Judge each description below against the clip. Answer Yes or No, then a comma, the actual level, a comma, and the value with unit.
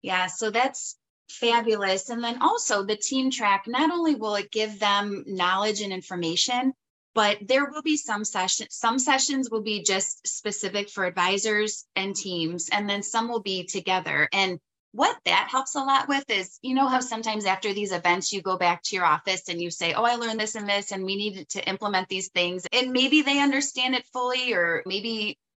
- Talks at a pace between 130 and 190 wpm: No, average, 200 wpm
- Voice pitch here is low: No, high, 210 Hz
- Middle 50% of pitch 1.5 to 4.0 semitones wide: No, average, 4.5 semitones